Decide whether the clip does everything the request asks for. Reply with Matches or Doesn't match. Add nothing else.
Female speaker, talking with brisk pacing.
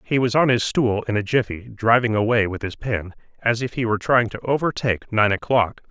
Doesn't match